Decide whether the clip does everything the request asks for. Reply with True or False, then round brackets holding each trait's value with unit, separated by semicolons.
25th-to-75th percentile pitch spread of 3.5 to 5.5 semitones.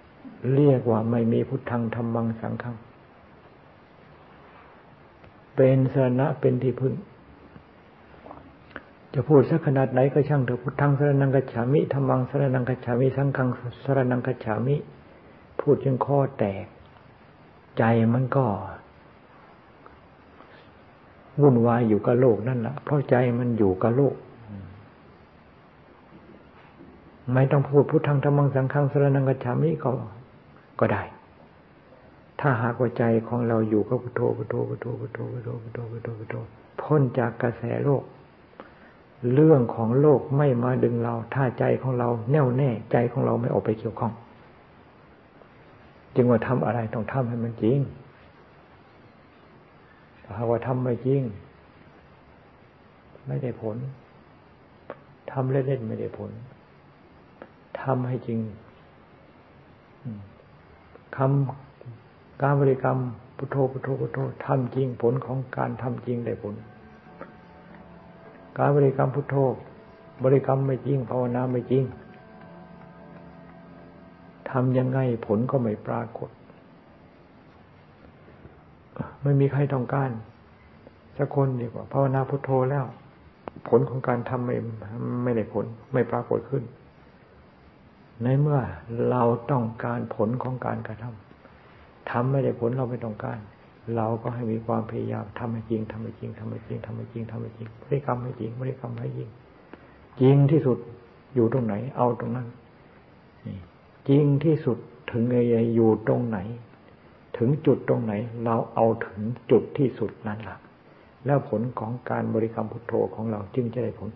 False (2.8 semitones)